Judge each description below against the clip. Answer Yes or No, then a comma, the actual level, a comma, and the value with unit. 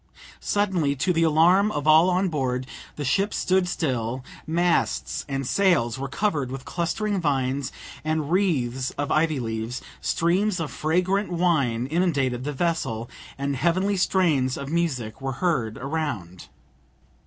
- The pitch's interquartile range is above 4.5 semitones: Yes, average, 5.3 semitones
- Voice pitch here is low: No, medium, 155 Hz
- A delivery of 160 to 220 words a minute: No, average, 140 wpm